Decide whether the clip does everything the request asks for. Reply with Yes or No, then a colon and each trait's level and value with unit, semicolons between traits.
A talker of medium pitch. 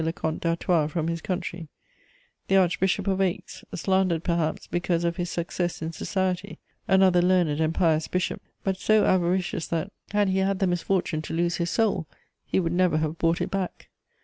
Yes: medium, 175 Hz